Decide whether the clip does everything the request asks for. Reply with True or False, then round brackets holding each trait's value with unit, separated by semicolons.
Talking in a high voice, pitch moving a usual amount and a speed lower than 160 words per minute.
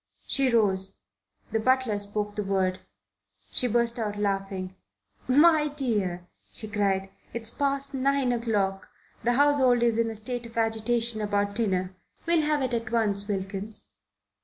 True (225 Hz; 3.7 semitones; 145 wpm)